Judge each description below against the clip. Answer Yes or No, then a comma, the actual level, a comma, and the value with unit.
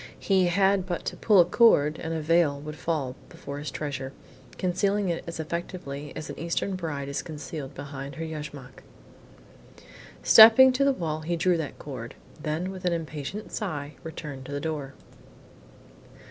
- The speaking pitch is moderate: Yes, medium, 160 Hz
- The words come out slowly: No, average, 165 wpm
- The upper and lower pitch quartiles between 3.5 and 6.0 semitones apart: Yes, average, 4.0 semitones